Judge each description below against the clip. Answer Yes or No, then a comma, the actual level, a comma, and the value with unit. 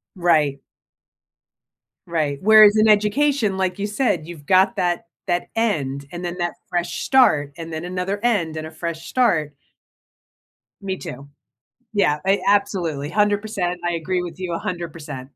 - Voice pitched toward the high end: No, medium, 175 Hz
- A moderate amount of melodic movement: Yes, average, 4.3 semitones